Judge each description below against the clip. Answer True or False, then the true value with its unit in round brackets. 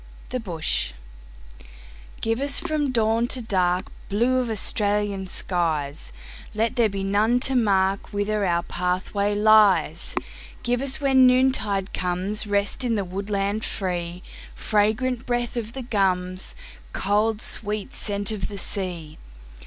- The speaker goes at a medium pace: False (110 wpm)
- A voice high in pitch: True (205 Hz)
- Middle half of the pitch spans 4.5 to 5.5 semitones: False (3.9 semitones)